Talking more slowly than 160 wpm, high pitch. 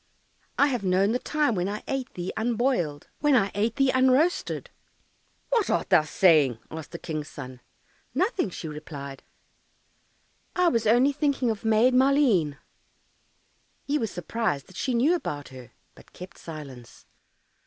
Yes: average, 150 wpm; high, 215 Hz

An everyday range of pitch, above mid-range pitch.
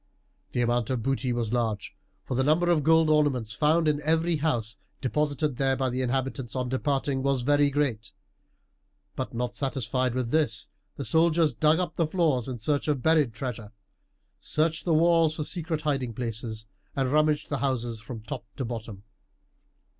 No: average, 4.1 semitones; low, 135 Hz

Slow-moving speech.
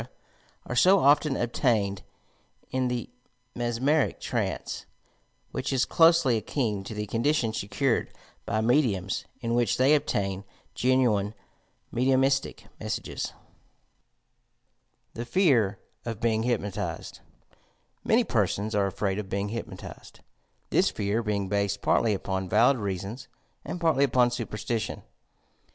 Yes: slow, 115 wpm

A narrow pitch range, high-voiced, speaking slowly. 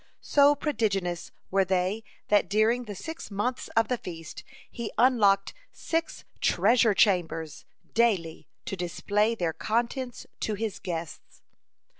No: average, 4.4 semitones; high, 210 Hz; slow, 125 wpm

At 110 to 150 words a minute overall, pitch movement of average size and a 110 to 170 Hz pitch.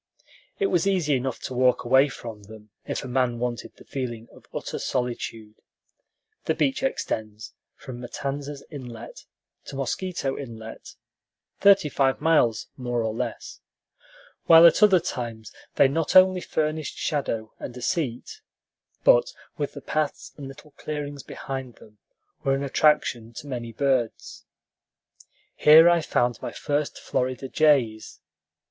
Yes: average, 140 wpm; average, 4.3 semitones; low, 135 Hz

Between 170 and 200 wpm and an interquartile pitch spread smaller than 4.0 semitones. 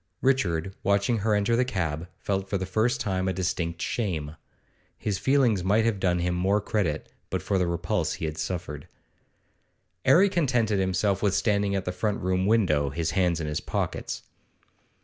Yes: average, 175 wpm; average, 3.5 semitones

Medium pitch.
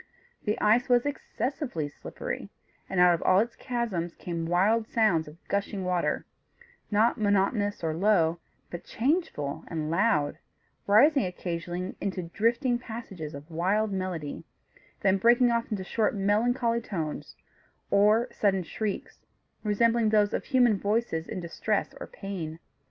No: high, 200 Hz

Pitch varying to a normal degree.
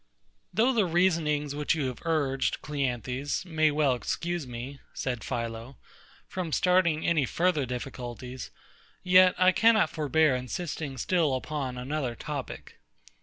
Yes: average, 4.9 semitones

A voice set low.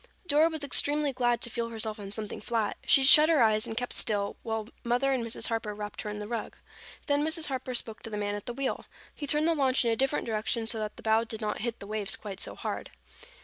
No: high, 230 Hz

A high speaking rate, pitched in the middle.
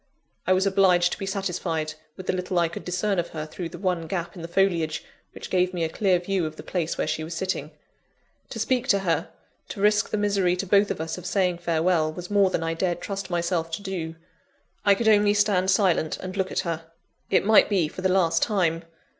Yes: fast, 230 wpm; medium, 180 Hz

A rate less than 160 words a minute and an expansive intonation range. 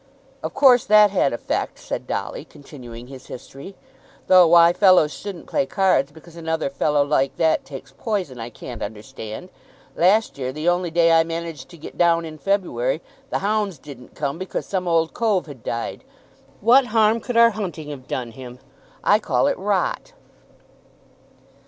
No: average, 165 wpm; wide, 5.8 semitones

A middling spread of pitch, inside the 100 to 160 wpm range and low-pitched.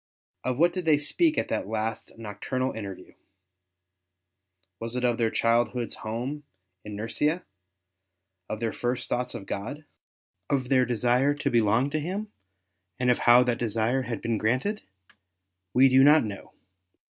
Yes: average, 3.7 semitones; average, 150 wpm; low, 125 Hz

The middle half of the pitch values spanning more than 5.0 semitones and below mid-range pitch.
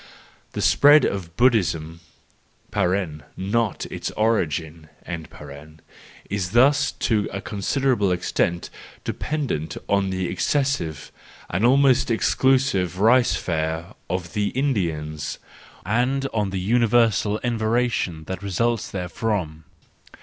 Yes: wide, 5.6 semitones; low, 100 Hz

